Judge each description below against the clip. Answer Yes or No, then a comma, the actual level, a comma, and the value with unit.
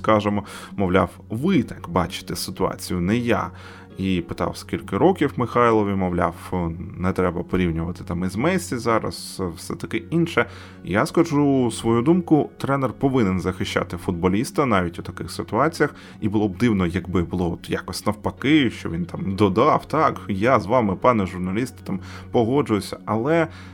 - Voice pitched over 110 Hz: No, low, 100 Hz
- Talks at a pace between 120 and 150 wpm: Yes, average, 145 wpm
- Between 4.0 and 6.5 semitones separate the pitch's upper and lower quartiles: Yes, average, 4.4 semitones